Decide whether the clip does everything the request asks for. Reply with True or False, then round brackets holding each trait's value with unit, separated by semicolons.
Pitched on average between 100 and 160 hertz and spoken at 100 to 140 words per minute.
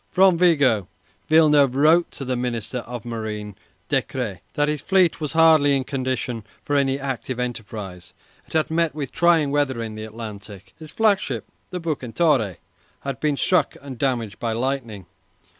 False (135 Hz; 160 wpm)